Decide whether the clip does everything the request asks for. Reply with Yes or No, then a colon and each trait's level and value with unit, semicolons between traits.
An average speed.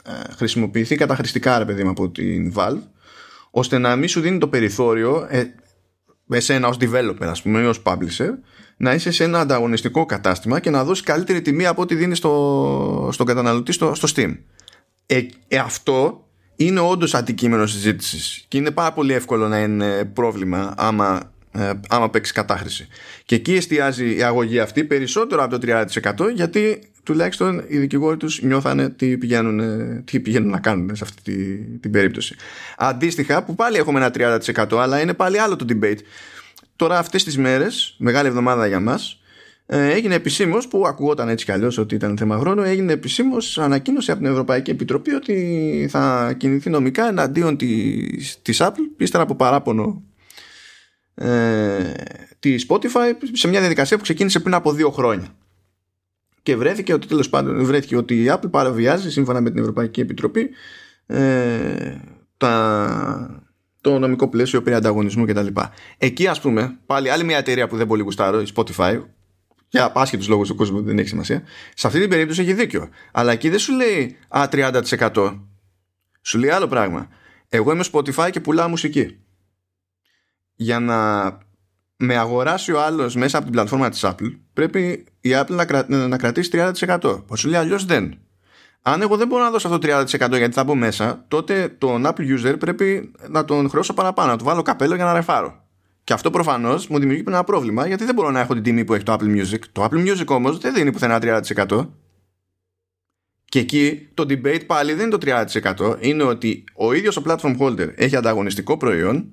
No: fast, 175 wpm